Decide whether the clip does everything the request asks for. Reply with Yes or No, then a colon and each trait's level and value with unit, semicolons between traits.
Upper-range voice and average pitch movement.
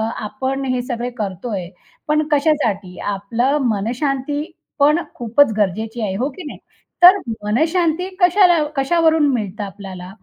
No: very high, 250 Hz; wide, 6.4 semitones